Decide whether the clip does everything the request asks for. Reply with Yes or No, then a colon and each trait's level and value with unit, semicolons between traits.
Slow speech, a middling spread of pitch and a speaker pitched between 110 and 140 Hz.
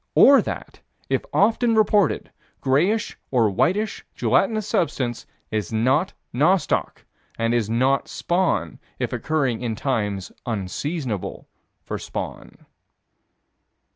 No: slow, 105 wpm; wide, 8.7 semitones; low, 135 Hz